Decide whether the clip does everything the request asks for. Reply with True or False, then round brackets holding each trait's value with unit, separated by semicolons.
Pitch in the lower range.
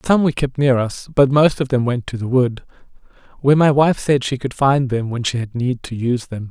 True (130 Hz)